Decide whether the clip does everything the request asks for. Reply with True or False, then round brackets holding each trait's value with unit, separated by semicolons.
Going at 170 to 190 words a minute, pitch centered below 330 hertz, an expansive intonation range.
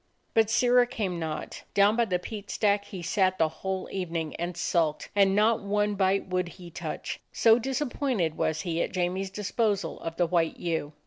False (185 wpm; 190 Hz; 3.5 semitones)